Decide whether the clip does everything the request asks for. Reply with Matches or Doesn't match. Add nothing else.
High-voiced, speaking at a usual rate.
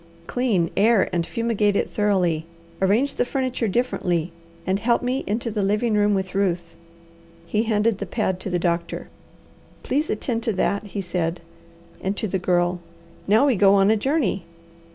Matches